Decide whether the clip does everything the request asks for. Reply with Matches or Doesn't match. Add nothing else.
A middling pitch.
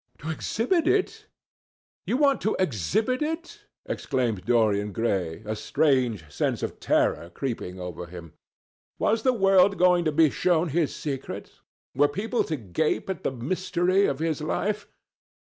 Matches